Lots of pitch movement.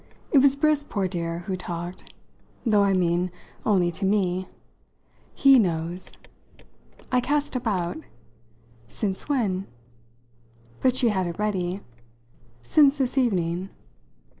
Yes: wide, 6.1 semitones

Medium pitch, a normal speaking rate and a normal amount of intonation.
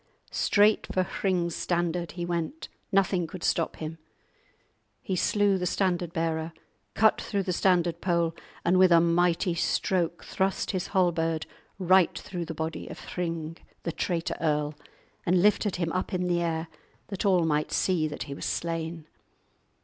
No: medium, 175 Hz; average, 155 wpm; narrow, 2.2 semitones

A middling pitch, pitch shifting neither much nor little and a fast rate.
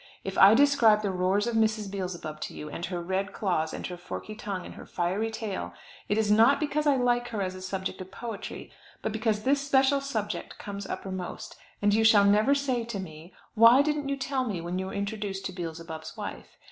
No: high, 205 Hz; average, 4.2 semitones; fast, 215 wpm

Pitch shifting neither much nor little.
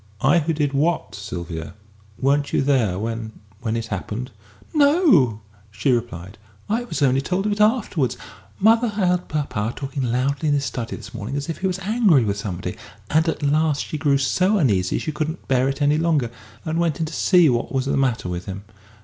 No: wide, 6.3 semitones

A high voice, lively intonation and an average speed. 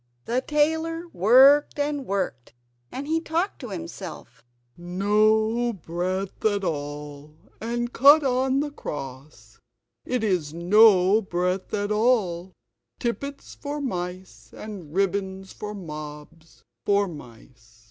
No: high, 200 Hz; wide, 7.0 semitones; slow, 115 wpm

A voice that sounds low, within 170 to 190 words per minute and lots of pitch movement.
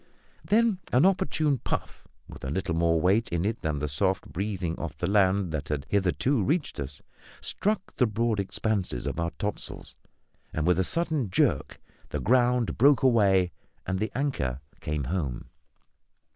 No: very low, 95 Hz; average, 160 wpm; wide, 7.0 semitones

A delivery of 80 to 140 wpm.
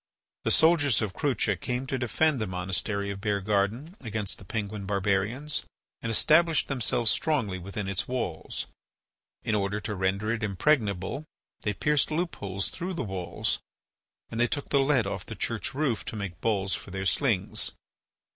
No: average, 165 wpm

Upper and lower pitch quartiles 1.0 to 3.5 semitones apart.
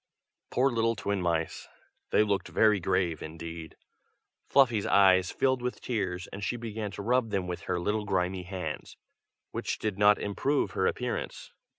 No: average, 3.9 semitones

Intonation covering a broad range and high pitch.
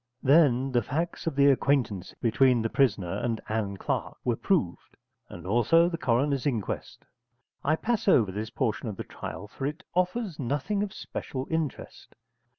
No: wide, 6.1 semitones; low, 135 Hz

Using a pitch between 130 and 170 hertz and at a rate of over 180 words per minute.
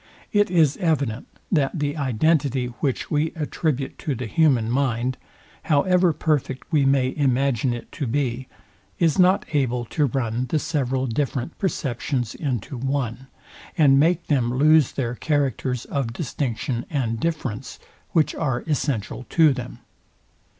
No: low, 135 Hz; slow, 135 wpm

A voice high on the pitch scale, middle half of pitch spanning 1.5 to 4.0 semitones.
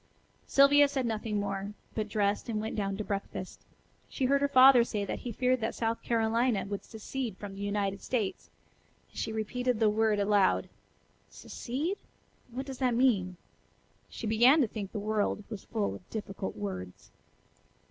Yes: high, 220 Hz; average, 3.6 semitones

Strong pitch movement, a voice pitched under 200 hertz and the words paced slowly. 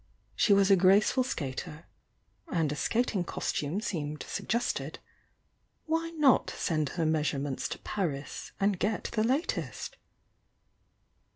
Yes: wide, 6.5 semitones; medium, 185 Hz; slow, 125 wpm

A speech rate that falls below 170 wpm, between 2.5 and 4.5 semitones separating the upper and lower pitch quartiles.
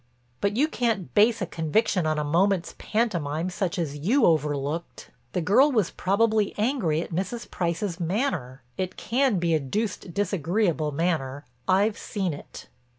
No: average, 150 wpm; average, 5.0 semitones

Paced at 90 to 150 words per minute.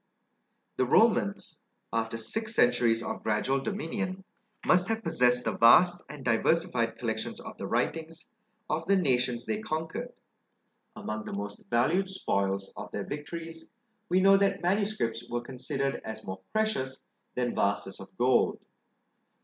Yes: average, 140 wpm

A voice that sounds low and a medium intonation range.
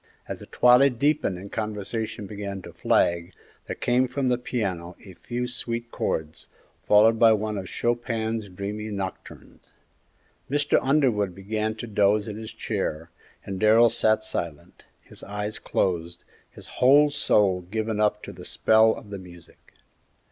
Yes: low, 110 Hz; average, 3.4 semitones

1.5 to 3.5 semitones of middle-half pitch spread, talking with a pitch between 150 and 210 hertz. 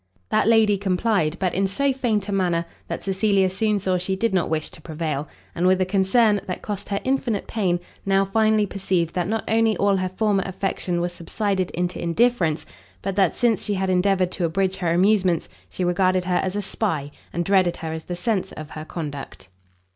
Yes: average, 2.7 semitones; high, 190 Hz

